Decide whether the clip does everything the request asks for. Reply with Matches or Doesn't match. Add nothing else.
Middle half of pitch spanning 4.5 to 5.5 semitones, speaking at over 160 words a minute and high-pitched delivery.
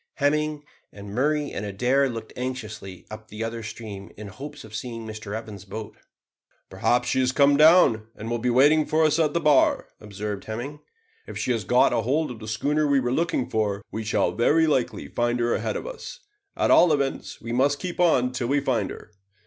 Doesn't match